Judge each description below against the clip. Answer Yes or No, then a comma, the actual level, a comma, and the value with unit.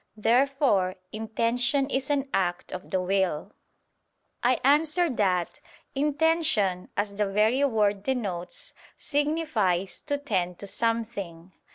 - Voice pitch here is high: Yes, high, 220 Hz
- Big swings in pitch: Yes, wide, 6.5 semitones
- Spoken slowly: Yes, slow, 110 wpm